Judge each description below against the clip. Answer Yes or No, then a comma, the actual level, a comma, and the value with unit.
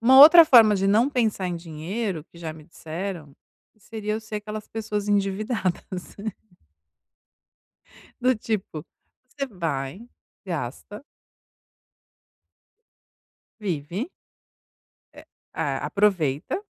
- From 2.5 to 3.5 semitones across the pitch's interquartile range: No, average, 4.6 semitones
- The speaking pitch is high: Yes, high, 200 Hz